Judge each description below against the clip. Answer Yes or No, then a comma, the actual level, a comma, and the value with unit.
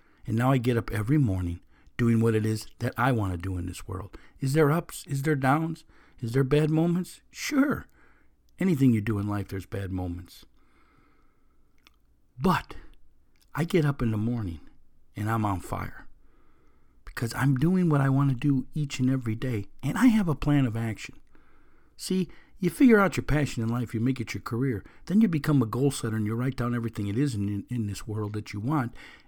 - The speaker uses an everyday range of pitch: No, wide, 5.9 semitones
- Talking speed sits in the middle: No, fast, 210 wpm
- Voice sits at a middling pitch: No, low, 120 Hz